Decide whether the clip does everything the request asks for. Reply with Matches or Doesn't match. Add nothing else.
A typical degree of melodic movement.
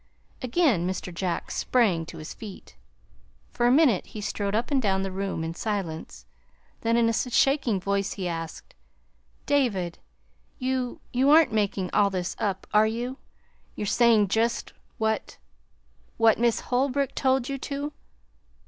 Matches